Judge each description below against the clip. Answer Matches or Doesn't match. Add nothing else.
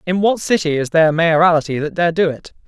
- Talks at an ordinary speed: Doesn't match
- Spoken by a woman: Doesn't match